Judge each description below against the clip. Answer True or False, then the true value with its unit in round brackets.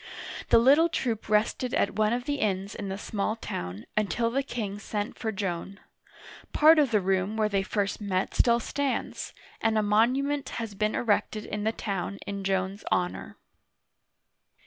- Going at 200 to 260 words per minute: False (170 wpm)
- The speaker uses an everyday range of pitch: True (3.0 semitones)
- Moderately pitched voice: False (215 Hz)